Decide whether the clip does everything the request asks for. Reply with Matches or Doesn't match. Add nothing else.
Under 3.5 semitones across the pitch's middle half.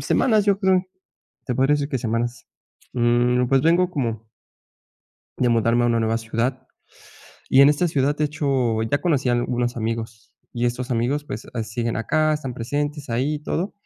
Doesn't match